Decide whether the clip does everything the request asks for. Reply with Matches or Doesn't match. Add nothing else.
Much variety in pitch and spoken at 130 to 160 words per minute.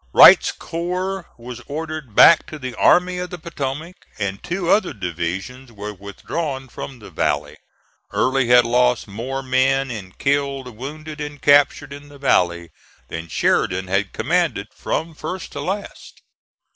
Matches